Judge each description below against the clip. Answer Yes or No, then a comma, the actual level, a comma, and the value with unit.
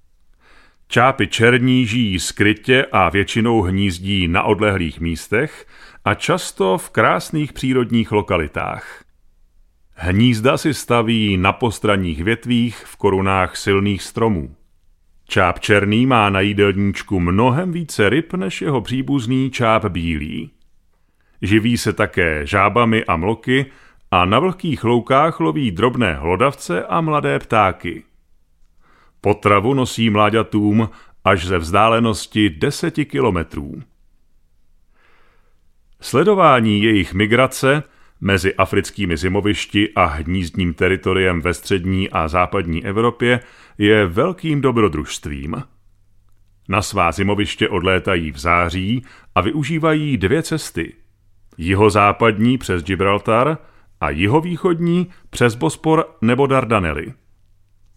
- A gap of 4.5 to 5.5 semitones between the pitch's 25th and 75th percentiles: Yes, average, 4.9 semitones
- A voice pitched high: No, low, 105 Hz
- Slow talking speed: Yes, slow, 100 wpm